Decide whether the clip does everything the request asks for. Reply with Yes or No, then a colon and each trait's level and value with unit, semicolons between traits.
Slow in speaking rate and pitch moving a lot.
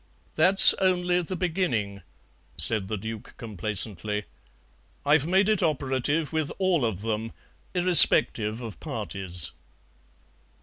Yes: slow, 105 wpm; wide, 8.8 semitones